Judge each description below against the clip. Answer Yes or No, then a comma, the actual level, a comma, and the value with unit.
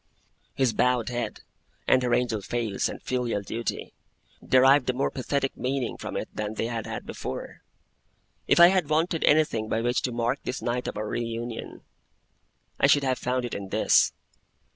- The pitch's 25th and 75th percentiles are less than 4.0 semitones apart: Yes, narrow, 2.6 semitones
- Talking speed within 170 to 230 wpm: Yes, average, 180 wpm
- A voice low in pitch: Yes, low, 125 Hz